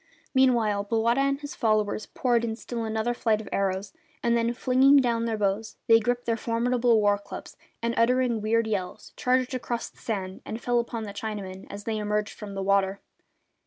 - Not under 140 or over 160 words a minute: No, average, 190 wpm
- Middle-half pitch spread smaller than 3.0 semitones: Yes, narrow, 2.6 semitones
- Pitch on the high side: Yes, high, 225 Hz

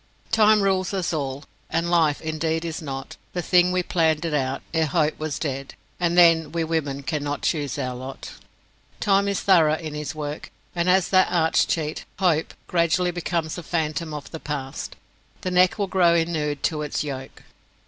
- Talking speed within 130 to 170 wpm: No, average, 180 wpm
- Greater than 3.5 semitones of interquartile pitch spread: No, average, 2.8 semitones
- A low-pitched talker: No, medium, 160 Hz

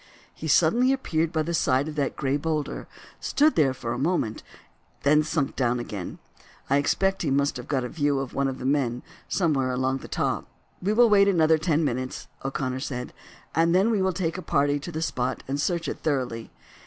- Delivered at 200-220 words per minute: Yes, fast, 205 wpm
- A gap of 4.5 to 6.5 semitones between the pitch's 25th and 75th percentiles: No, average, 4.1 semitones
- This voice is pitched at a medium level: Yes, medium, 145 Hz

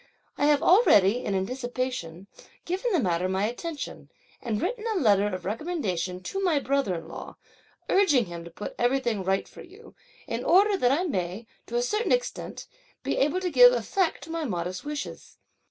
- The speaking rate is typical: Yes, average, 180 wpm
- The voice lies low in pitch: No, very high, 250 Hz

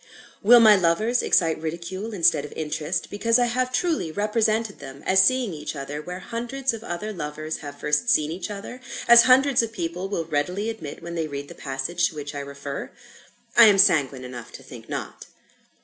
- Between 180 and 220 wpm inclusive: Yes, average, 195 wpm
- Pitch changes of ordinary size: No, wide, 7.2 semitones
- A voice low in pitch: No, medium, 180 Hz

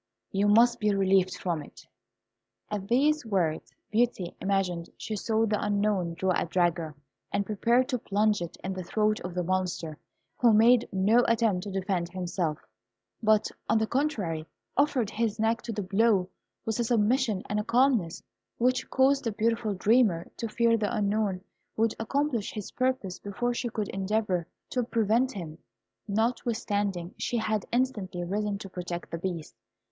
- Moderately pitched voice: No, high, 210 Hz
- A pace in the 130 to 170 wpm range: Yes, average, 160 wpm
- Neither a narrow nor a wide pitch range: Yes, average, 3.8 semitones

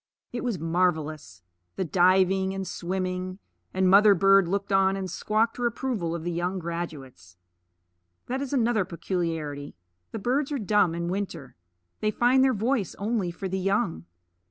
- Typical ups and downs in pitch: Yes, average, 3.8 semitones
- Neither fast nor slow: Yes, average, 155 wpm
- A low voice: No, high, 190 Hz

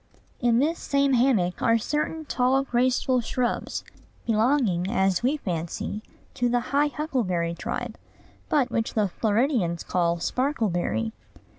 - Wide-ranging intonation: Yes, wide, 6.6 semitones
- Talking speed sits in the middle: No, slow, 125 wpm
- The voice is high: Yes, high, 240 Hz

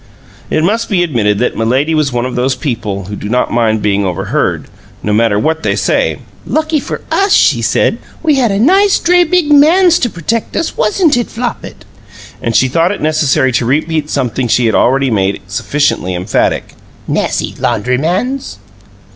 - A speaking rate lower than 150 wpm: No, average, 175 wpm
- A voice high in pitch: No, medium, 145 Hz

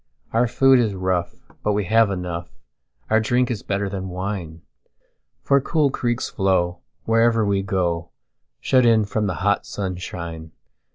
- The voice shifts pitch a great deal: No, average, 4.1 semitones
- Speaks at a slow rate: Yes, slow, 130 wpm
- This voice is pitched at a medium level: No, low, 100 Hz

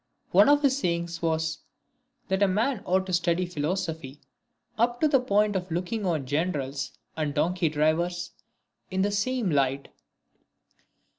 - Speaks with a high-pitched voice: No, medium, 180 Hz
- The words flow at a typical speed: Yes, average, 150 wpm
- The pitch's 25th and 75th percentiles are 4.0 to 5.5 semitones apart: Yes, average, 4.4 semitones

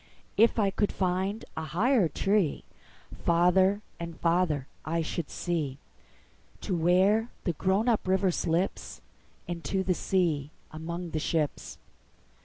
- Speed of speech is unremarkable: No, slow, 110 wpm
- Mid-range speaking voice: Yes, medium, 180 Hz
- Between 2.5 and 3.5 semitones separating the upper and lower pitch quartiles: Yes, average, 2.9 semitones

